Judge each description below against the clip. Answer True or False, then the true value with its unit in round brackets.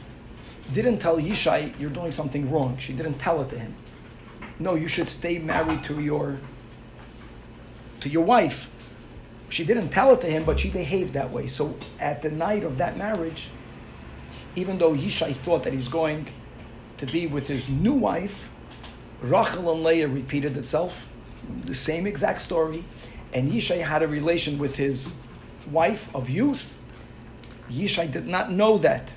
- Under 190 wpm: True (160 wpm)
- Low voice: False (155 Hz)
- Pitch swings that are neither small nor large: True (3.9 semitones)